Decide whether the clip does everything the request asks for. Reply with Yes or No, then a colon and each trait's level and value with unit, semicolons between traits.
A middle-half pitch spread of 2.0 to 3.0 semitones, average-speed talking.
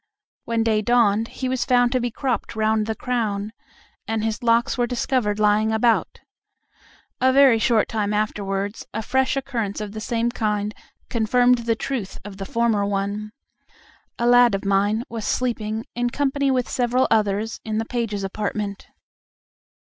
Yes: average, 2.7 semitones; average, 160 wpm